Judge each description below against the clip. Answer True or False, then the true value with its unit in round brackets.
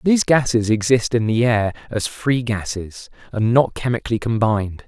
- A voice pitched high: False (115 Hz)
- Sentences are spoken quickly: False (160 wpm)